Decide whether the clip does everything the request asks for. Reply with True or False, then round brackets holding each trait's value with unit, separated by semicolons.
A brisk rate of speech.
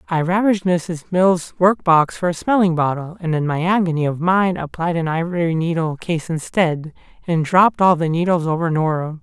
False (190 wpm)